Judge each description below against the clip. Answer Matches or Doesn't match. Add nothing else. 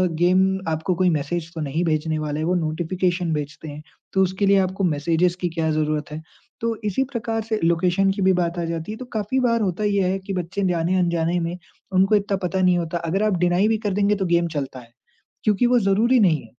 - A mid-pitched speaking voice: Matches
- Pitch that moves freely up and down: Doesn't match